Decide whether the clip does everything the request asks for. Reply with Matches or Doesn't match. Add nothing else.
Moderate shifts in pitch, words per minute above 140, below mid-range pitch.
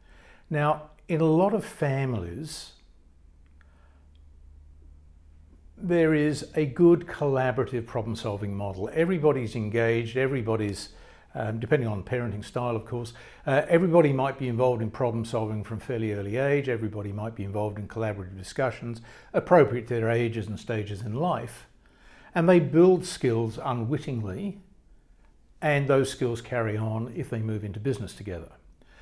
Doesn't match